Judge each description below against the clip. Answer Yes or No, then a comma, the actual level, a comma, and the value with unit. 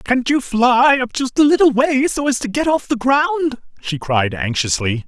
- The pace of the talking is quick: Yes, fast, 215 wpm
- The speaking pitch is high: Yes, high, 235 Hz